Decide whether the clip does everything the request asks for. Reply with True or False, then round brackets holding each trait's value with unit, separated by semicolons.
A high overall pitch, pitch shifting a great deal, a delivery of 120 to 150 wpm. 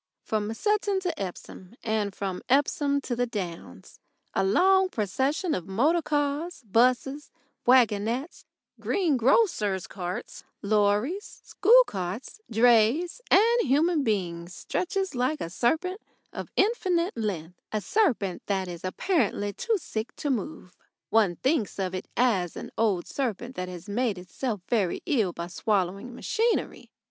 True (235 Hz; 8.1 semitones; 135 wpm)